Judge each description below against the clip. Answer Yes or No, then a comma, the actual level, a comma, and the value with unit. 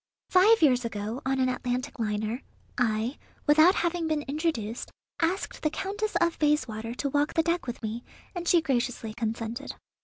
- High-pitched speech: Yes, very high, 270 Hz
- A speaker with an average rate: Yes, average, 160 wpm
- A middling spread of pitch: No, wide, 6.0 semitones